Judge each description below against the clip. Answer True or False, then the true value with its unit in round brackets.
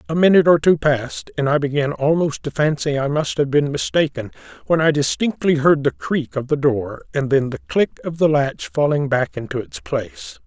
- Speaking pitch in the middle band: True (145 Hz)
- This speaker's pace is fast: True (210 wpm)